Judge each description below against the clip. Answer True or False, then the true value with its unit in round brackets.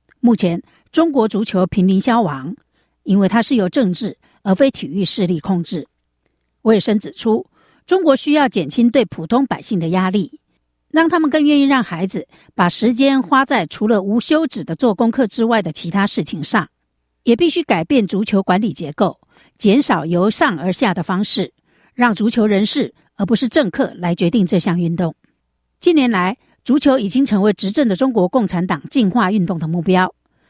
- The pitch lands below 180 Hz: False (215 Hz)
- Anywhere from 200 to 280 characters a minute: True (270 characters per minute)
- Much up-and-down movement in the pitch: True (5.7 semitones)